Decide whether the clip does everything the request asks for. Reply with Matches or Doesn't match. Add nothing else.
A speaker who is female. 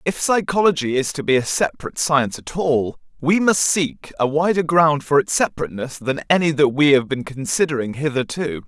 Doesn't match